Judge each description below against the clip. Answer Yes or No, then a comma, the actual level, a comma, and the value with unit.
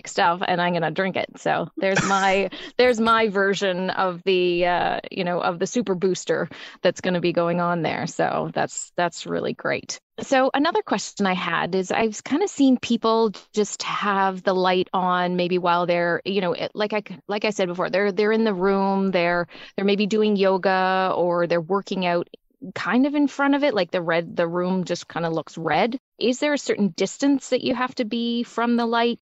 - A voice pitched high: Yes, high, 195 Hz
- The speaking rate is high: Yes, fast, 210 wpm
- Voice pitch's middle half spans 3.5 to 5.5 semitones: Yes, average, 4.1 semitones